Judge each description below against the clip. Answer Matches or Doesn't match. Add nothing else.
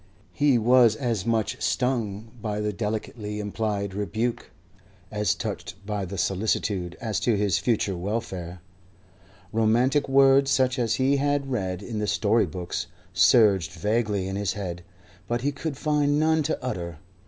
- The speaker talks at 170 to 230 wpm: Doesn't match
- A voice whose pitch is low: Matches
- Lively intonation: Doesn't match